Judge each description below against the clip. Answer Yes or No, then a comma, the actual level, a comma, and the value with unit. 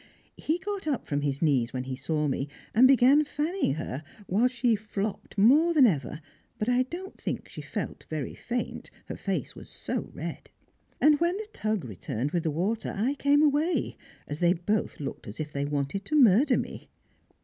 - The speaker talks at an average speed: Yes, average, 190 wpm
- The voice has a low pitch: No, high, 215 Hz